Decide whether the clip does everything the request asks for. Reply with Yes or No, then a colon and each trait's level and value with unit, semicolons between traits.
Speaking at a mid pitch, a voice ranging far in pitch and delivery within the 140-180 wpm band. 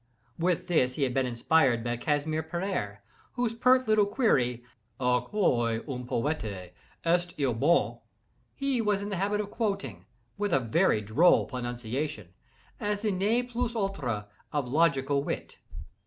Yes: medium, 155 Hz; wide, 8.6 semitones; average, 150 wpm